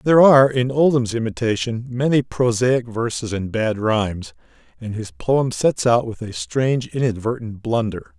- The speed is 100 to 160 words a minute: Yes, average, 155 wpm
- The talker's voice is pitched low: Yes, low, 120 Hz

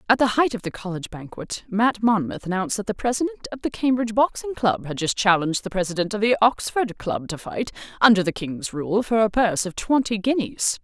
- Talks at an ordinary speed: No, fast, 215 wpm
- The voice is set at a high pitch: Yes, high, 215 Hz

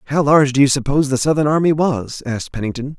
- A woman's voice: No, male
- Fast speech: Yes, fast, 220 wpm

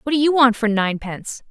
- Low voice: No, high, 245 Hz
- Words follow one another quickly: Yes, fast, 240 wpm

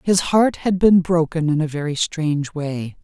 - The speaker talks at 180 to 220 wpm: Yes, average, 200 wpm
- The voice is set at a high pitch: No, medium, 160 Hz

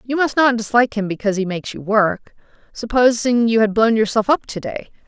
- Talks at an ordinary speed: No, fast, 215 wpm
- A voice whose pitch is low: No, high, 225 Hz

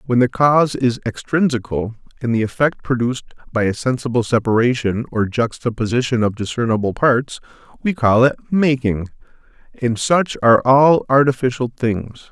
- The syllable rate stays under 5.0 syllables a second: No, 5.2 syllables/s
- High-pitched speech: No, low, 125 Hz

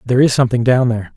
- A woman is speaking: No, male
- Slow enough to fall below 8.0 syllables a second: No, 8.7 syllables/s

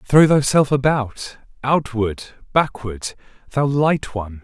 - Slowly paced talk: Yes, slow, 95 wpm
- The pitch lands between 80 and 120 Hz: No, low, 130 Hz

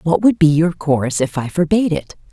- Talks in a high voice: No, medium, 165 Hz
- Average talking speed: No, fast, 235 wpm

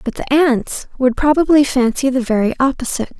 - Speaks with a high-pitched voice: Yes, very high, 260 Hz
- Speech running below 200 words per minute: Yes, average, 170 wpm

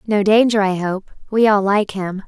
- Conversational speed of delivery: No, fast, 210 wpm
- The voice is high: Yes, high, 205 Hz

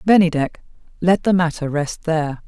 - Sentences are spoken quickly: No, average, 145 wpm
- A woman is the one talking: Yes, female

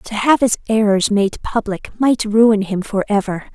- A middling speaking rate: Yes, average, 185 wpm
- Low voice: No, high, 215 Hz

